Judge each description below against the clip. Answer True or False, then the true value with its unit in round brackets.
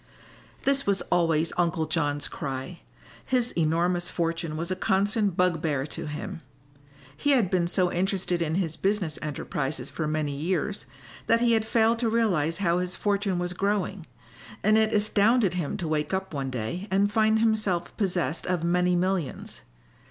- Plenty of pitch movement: False (4.0 semitones)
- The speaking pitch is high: False (180 Hz)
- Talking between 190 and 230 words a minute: False (160 wpm)